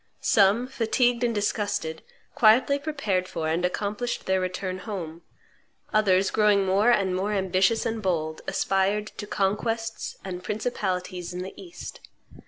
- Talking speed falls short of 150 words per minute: Yes, slow, 135 wpm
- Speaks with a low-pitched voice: No, high, 200 Hz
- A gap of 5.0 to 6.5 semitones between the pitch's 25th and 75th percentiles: No, average, 3.3 semitones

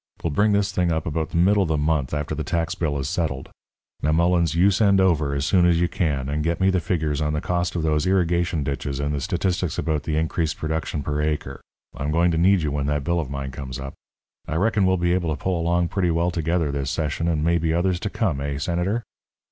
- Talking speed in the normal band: No, fast, 245 wpm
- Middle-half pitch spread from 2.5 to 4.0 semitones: Yes, average, 3.0 semitones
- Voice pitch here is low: Yes, very low, 80 Hz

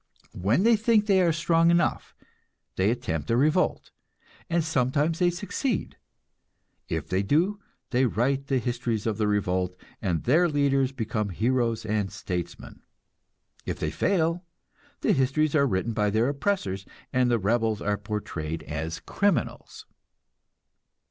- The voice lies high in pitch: No, low, 125 Hz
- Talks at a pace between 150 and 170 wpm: No, average, 140 wpm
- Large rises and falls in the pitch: Yes, wide, 7.5 semitones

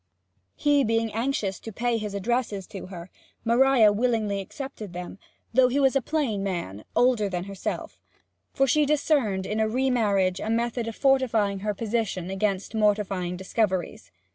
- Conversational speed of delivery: Yes, average, 160 wpm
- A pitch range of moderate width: Yes, average, 4.1 semitones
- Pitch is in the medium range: No, high, 215 Hz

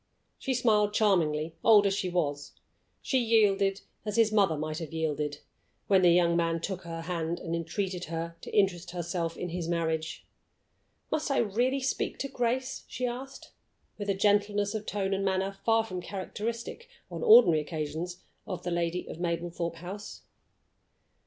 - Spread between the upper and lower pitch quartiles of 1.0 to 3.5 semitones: No, average, 3.9 semitones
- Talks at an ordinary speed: Yes, average, 165 wpm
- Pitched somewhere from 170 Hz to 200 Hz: Yes, medium, 185 Hz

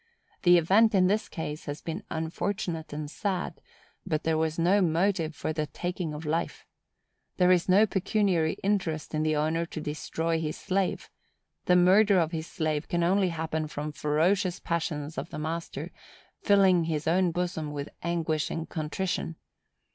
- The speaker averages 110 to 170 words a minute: Yes, average, 160 wpm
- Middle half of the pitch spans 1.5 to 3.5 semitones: Yes, average, 2.8 semitones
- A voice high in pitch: No, medium, 165 Hz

